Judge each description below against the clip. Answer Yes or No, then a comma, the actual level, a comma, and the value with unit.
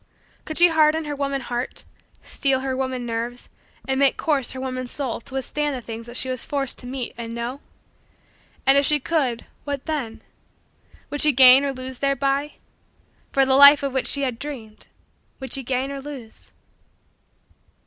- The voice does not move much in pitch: Yes, narrow, 2.1 semitones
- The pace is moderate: Yes, average, 180 wpm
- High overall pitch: Yes, very high, 265 Hz